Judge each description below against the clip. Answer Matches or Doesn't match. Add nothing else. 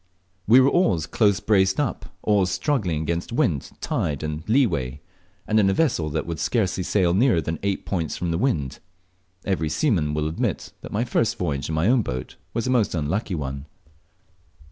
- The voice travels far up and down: Matches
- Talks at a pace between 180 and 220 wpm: Matches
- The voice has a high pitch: Doesn't match